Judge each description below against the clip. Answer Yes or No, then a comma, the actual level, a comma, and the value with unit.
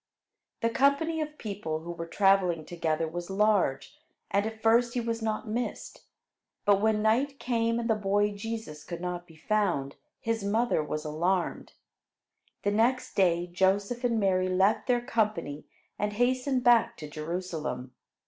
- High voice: Yes, high, 205 Hz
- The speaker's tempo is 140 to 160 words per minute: Yes, average, 155 wpm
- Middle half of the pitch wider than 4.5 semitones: Yes, average, 4.9 semitones